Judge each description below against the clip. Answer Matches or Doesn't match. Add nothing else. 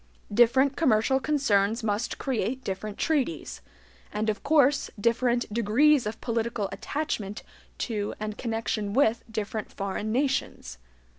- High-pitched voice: Matches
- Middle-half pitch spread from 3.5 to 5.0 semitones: Matches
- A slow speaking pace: Matches